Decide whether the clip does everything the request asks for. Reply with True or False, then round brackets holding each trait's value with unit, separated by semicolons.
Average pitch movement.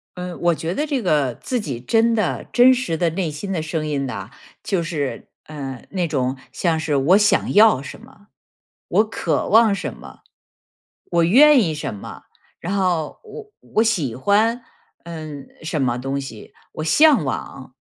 False (7.1 semitones)